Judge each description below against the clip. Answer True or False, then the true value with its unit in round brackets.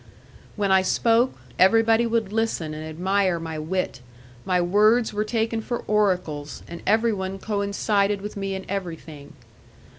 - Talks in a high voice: True (200 Hz)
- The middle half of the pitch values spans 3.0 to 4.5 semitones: True (3.7 semitones)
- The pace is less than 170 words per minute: True (140 wpm)